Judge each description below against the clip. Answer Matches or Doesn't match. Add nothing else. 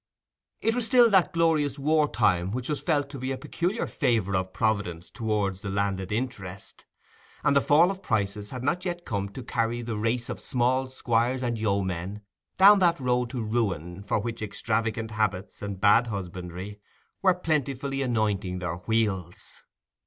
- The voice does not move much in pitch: Doesn't match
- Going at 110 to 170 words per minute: Matches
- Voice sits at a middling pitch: Doesn't match